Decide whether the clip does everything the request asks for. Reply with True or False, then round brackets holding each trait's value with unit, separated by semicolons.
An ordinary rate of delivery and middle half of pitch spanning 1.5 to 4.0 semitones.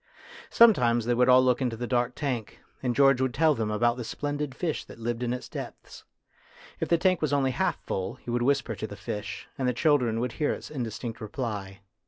False (220 wpm; 3.0 semitones)